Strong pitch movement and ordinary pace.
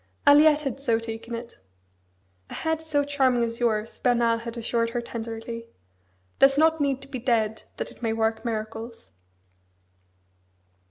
No: average, 3.1 semitones; average, 150 wpm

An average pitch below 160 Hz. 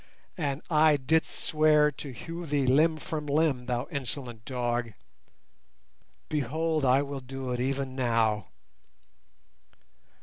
Yes: medium, 140 Hz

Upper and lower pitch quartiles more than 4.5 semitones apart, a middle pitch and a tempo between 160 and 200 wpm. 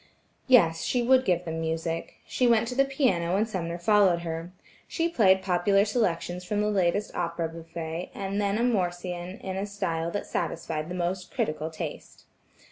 No: average, 3.7 semitones; medium, 180 Hz; average, 175 wpm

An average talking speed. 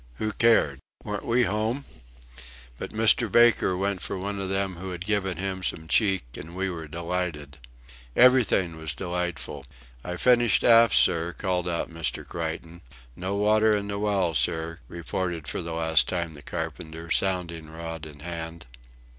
Yes: average, 160 wpm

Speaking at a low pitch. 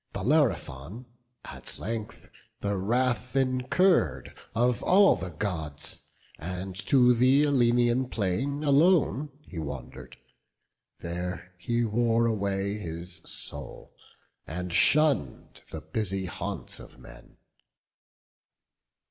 Yes: low, 115 Hz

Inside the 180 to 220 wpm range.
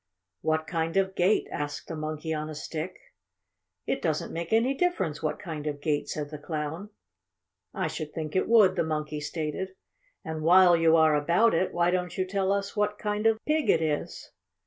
Yes: average, 190 wpm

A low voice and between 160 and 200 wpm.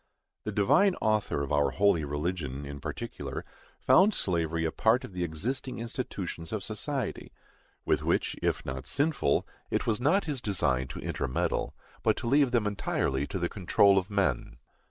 Yes: low, 100 Hz; average, 165 wpm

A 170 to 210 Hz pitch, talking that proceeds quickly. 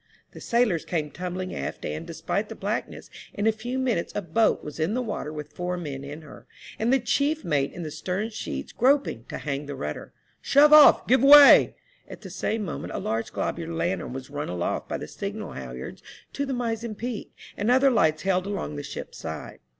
Yes: medium, 185 Hz; fast, 215 wpm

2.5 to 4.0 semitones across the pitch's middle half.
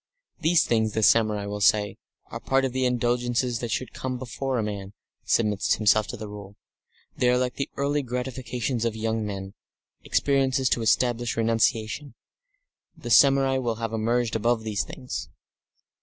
Yes: average, 2.8 semitones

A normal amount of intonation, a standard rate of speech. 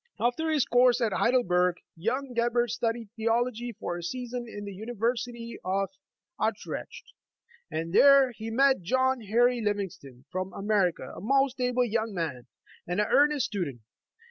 Yes: average, 4.2 semitones; average, 150 wpm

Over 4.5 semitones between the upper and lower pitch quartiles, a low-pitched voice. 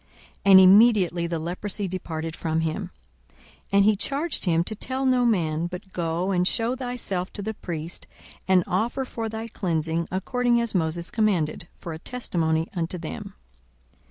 No: average, 5.0 semitones; medium, 185 Hz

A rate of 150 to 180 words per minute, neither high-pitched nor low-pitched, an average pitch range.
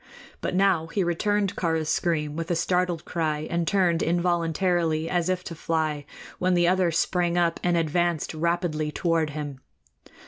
No: average, 160 wpm; medium, 170 Hz; narrow, 1.9 semitones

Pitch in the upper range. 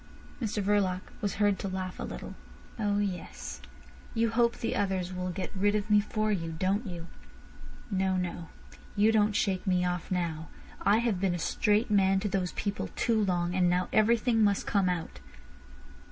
Yes: high, 195 Hz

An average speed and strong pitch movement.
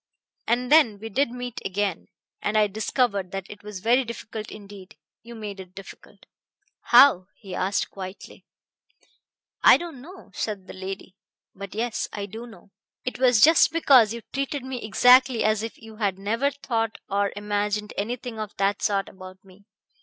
No: average, 170 wpm; average, 3.6 semitones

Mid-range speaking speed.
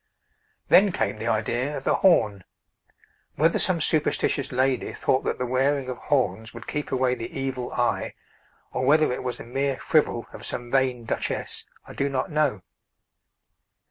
Yes: average, 165 wpm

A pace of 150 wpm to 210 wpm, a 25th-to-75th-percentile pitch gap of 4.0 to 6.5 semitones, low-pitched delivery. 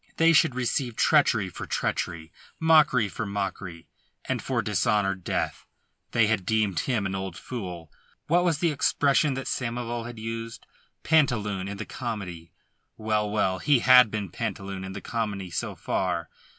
Yes: average, 155 wpm; average, 4.7 semitones; low, 110 Hz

